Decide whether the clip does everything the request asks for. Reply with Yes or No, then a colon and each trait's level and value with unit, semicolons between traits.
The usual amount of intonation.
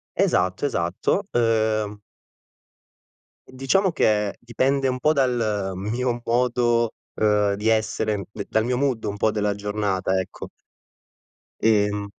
Yes: average, 3.2 semitones